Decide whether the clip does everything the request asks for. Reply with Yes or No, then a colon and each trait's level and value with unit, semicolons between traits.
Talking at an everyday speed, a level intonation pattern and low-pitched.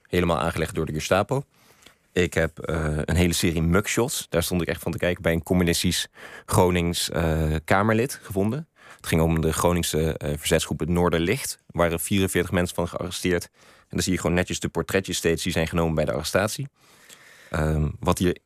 Yes: average, 190 wpm; narrow, 2.0 semitones; very low, 85 Hz